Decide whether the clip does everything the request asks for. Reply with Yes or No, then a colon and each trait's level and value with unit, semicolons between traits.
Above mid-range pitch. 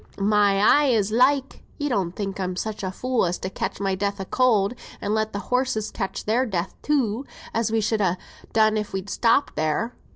Yes: high, 215 Hz